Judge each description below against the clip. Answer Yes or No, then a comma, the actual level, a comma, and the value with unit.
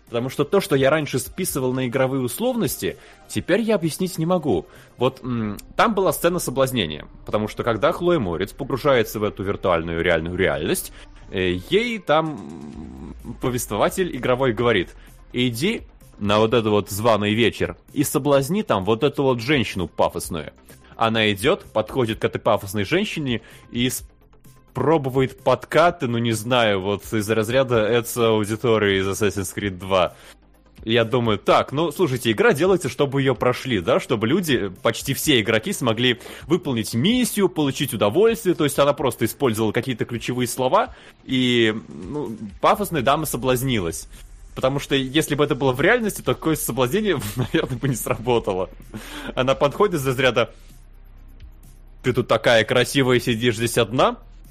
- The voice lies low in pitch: Yes, low, 125 Hz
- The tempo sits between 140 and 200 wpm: Yes, average, 150 wpm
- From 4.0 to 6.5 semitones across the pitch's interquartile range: Yes, average, 4.7 semitones